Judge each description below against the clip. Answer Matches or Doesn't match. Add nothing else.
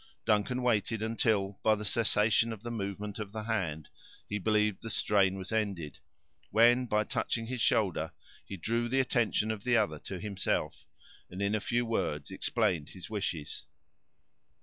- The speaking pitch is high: Doesn't match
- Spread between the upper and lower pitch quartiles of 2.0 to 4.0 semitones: Matches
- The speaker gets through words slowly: Doesn't match